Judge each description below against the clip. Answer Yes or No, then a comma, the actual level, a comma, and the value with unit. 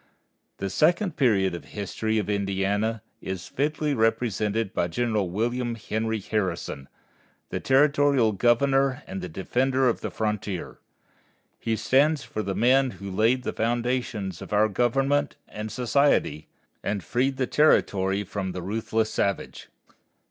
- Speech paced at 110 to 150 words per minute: Yes, average, 140 wpm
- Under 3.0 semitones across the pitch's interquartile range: No, average, 4.6 semitones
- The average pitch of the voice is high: No, low, 110 Hz